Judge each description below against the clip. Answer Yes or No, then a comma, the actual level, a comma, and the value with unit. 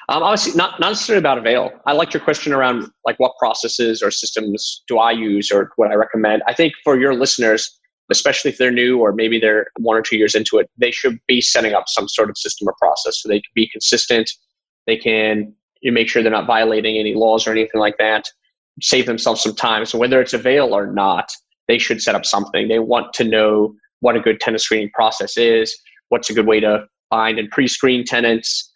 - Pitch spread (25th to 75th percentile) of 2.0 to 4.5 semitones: Yes, narrow, 2.6 semitones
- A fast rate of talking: Yes, fast, 225 wpm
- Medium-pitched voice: No, low, 115 Hz